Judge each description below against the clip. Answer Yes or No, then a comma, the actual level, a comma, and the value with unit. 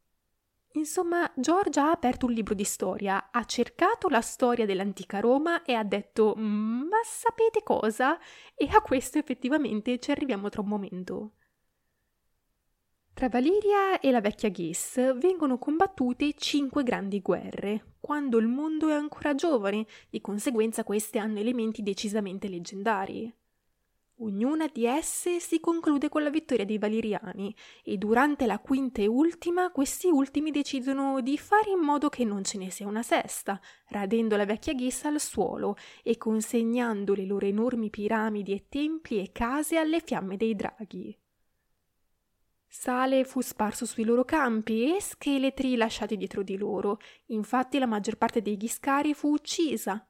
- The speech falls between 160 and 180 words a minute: No, average, 145 wpm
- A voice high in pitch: Yes, high, 240 Hz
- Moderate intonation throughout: No, wide, 5.8 semitones